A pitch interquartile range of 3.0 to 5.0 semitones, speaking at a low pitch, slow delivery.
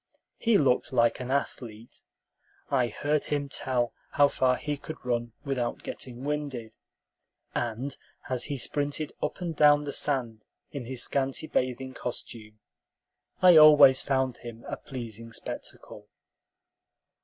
Yes: average, 3.3 semitones; low, 130 Hz; slow, 130 wpm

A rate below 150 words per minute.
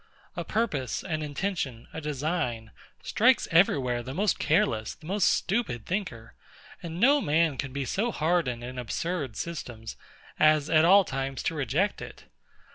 No: average, 155 wpm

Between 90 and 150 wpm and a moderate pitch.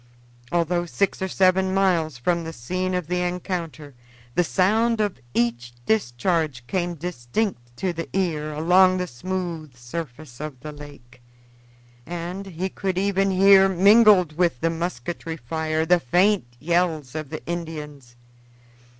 Yes: average, 140 wpm; medium, 170 Hz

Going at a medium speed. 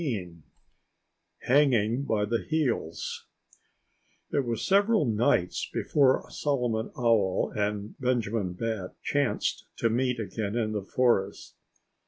No: slow, 110 wpm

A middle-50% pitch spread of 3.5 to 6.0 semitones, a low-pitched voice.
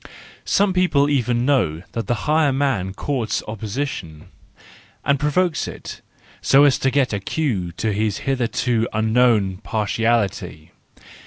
Yes: average, 5.1 semitones; low, 120 Hz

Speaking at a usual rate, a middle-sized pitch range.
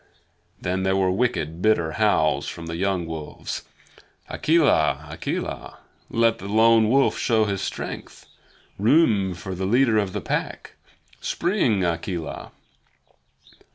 No: slow, 120 wpm; average, 5.0 semitones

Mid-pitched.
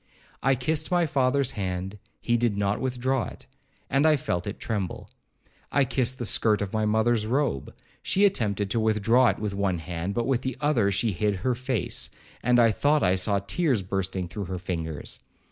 No: low, 110 Hz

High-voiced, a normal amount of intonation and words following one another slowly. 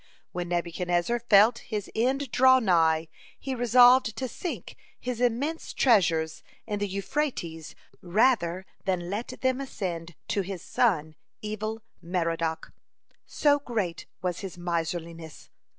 No: high, 200 Hz; wide, 6.1 semitones; slow, 120 wpm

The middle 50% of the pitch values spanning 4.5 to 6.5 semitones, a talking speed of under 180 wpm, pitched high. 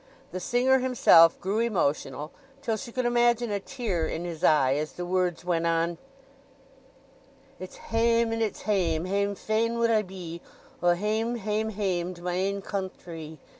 Yes: average, 4.8 semitones; average, 165 wpm; high, 195 Hz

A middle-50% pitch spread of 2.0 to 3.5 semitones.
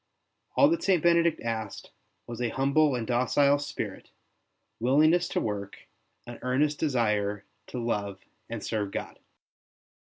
No: average, 5.2 semitones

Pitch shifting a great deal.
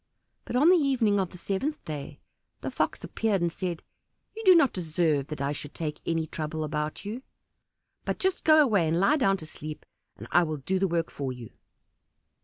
Yes: wide, 6.5 semitones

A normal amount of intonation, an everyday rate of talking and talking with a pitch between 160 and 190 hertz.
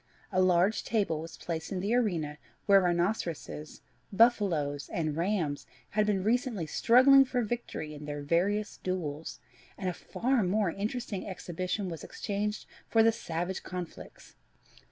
Yes: average, 4.4 semitones; average, 145 wpm; medium, 185 Hz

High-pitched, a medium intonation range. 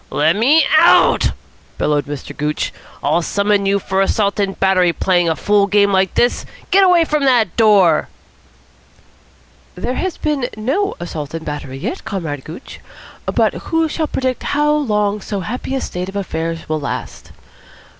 No: high, 200 Hz; wide, 7.3 semitones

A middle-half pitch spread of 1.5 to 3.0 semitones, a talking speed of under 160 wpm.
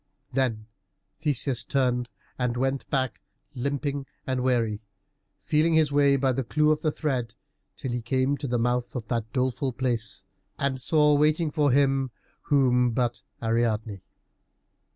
Yes: average, 2.7 semitones; average, 140 wpm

